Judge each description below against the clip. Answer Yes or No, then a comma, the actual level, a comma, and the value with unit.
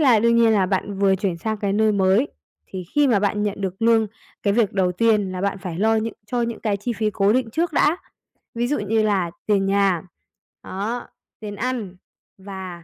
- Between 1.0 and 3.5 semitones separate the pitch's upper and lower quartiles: Yes, average, 2.9 semitones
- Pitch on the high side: Yes, high, 205 Hz